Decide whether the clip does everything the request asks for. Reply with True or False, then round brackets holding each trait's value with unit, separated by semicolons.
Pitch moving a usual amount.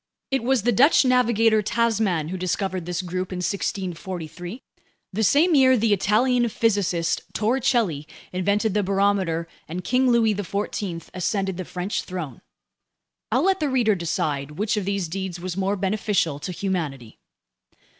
True (4.2 semitones)